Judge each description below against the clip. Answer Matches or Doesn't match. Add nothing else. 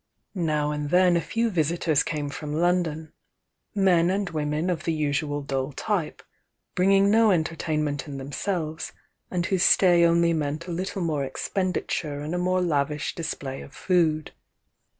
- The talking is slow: Doesn't match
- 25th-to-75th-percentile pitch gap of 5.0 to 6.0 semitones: Doesn't match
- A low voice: Doesn't match